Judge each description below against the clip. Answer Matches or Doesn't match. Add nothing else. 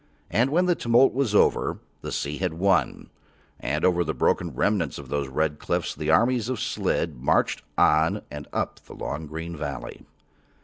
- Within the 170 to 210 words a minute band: Matches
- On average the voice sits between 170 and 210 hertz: Doesn't match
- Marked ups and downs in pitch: Matches